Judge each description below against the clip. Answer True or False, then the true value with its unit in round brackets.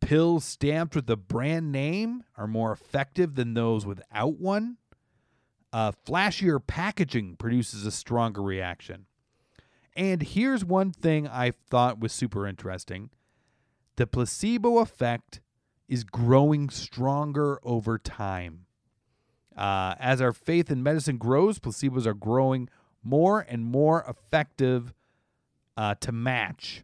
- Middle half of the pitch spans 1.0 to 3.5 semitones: False (5.1 semitones)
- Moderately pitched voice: False (125 Hz)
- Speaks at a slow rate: True (120 wpm)